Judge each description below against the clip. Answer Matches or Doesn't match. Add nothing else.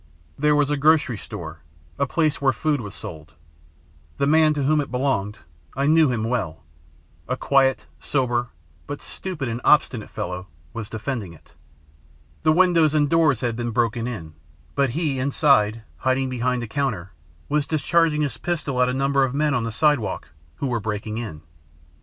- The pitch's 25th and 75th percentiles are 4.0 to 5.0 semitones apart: Matches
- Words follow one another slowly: Doesn't match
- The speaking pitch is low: Matches